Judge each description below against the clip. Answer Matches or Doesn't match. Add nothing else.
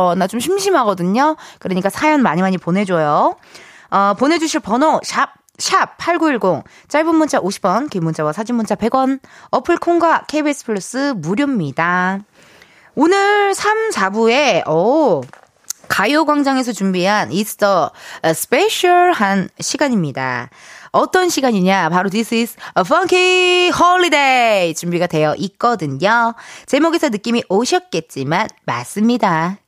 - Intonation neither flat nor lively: Doesn't match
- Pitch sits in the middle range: Doesn't match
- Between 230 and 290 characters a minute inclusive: Matches